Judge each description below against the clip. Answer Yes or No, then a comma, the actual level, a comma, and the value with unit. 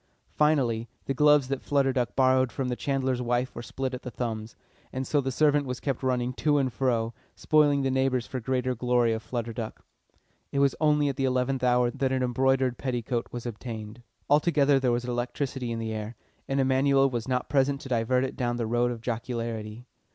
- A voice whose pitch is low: Yes, low, 125 Hz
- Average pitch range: No, narrow, 2.1 semitones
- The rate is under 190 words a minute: No, fast, 205 wpm